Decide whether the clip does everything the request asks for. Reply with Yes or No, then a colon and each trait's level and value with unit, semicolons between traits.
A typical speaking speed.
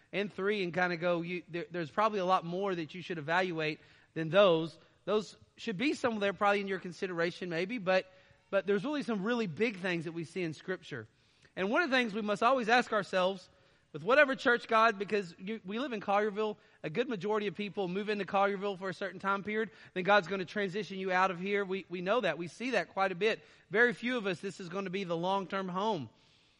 No: fast, 245 wpm